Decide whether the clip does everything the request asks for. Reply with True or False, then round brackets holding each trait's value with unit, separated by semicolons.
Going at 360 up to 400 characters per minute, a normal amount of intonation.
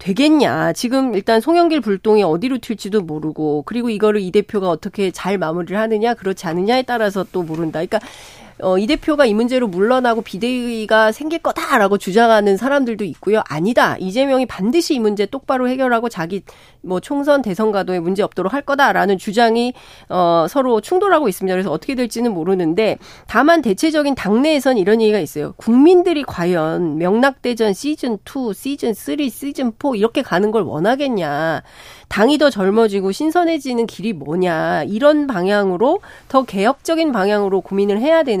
False (380 characters per minute; 5.9 semitones)